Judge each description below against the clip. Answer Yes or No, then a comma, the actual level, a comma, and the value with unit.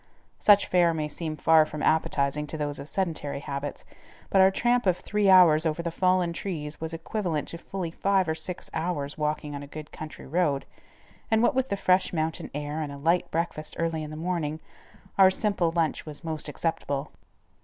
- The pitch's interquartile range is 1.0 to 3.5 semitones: Yes, average, 3.2 semitones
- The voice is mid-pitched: Yes, medium, 160 Hz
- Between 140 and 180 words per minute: No, average, 195 wpm